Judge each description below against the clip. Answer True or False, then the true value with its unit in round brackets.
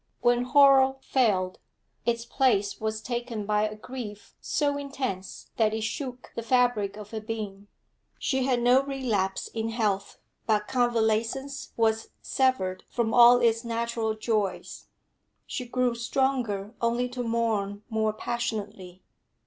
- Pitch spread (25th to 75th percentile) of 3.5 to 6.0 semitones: False (2.7 semitones)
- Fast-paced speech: False (135 wpm)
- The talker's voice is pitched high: True (230 Hz)